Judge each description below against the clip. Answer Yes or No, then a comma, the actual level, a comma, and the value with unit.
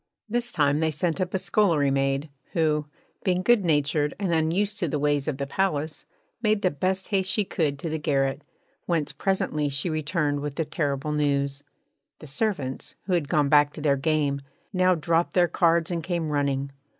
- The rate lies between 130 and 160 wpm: No, average, 185 wpm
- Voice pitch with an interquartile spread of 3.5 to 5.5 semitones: Yes, average, 4.0 semitones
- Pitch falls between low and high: Yes, medium, 155 Hz